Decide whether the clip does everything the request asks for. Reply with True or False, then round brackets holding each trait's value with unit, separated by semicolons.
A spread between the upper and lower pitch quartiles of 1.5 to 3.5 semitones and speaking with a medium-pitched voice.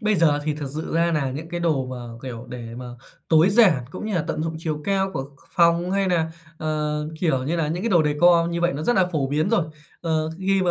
True (2.9 semitones; 160 Hz)